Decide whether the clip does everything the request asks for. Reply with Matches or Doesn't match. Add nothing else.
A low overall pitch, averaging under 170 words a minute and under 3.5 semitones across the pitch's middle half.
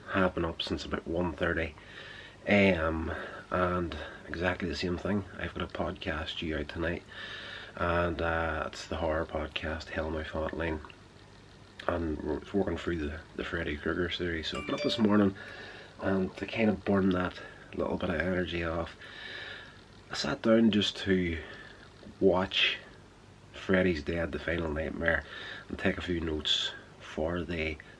Matches